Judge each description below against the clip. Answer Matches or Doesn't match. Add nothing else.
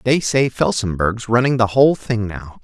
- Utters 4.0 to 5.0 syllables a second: Matches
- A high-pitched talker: Doesn't match